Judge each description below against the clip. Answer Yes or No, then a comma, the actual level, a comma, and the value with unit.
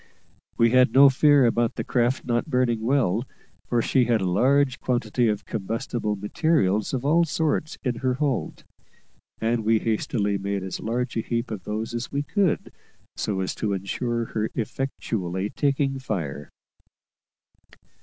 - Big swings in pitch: No, average, 3.7 semitones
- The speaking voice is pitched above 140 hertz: No, low, 120 Hz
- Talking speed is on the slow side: No, average, 155 wpm